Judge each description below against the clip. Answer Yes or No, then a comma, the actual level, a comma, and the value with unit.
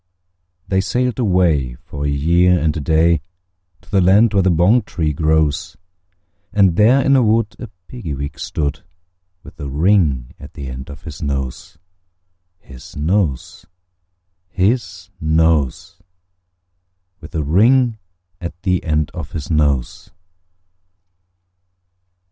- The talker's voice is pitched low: Yes, very low, 85 Hz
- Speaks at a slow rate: Yes, slow, 130 wpm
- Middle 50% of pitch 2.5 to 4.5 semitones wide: No, average, 5.0 semitones